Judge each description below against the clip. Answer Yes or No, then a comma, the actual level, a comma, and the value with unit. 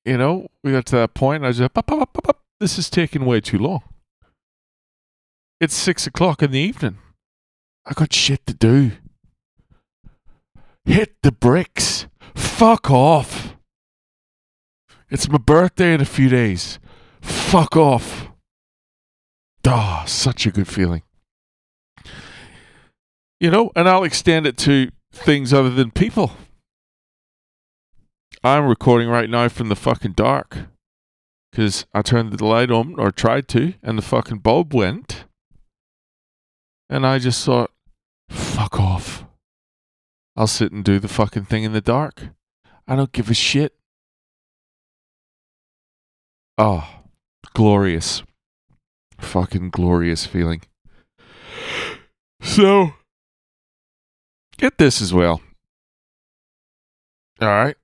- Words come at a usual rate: No, slow, 120 wpm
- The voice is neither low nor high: No, low, 120 Hz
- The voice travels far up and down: Yes, wide, 7.1 semitones